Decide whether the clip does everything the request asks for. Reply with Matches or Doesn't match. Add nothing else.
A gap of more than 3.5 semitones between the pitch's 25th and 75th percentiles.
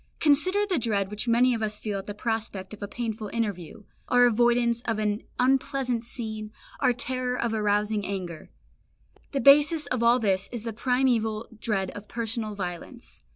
Doesn't match